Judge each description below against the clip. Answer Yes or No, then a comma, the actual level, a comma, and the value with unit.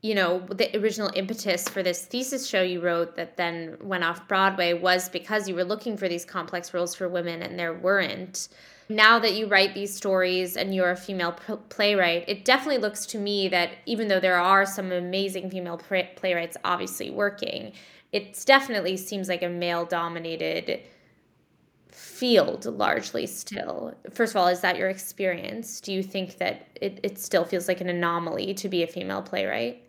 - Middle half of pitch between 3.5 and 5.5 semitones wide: No, narrow, 2.4 semitones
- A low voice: No, medium, 185 Hz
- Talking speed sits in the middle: Yes, average, 180 wpm